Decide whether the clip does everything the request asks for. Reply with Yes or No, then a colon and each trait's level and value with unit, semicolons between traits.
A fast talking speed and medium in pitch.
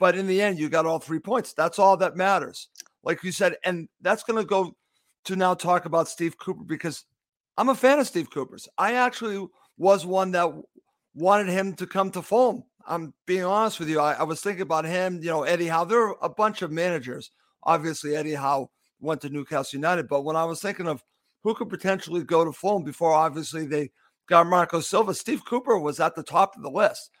Yes: fast, 220 wpm; medium, 175 Hz